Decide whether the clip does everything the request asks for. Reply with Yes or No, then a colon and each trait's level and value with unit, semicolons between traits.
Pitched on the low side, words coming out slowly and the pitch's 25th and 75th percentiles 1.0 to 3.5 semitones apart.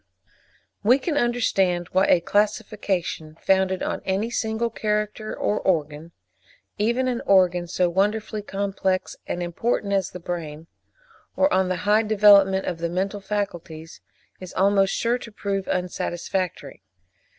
No: high, 195 Hz; slow, 130 wpm; average, 3.1 semitones